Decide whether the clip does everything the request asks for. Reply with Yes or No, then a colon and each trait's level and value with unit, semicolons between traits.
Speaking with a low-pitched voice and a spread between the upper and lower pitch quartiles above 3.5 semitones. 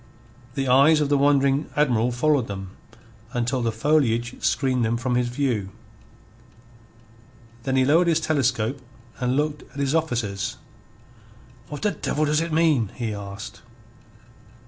Yes: low, 130 Hz; average, 4.0 semitones